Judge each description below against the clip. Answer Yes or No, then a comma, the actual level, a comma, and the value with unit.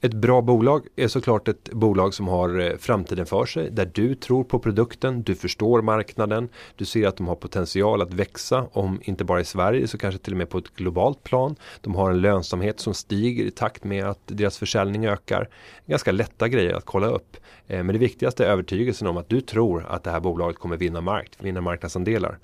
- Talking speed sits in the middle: No, fast, 210 wpm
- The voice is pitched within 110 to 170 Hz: No, low, 100 Hz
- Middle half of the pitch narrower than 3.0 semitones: No, average, 4.1 semitones